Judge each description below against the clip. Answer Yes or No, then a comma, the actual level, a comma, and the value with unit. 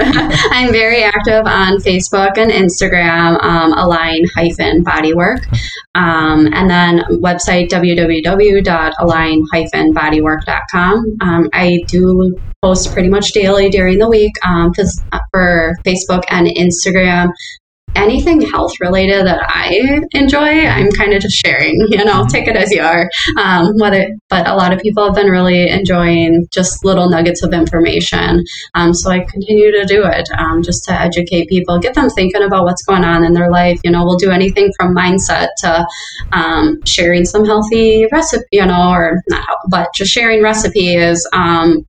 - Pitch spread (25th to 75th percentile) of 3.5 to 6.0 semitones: No, average, 2.9 semitones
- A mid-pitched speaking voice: Yes, medium, 180 Hz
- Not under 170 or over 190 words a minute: No, average, 155 wpm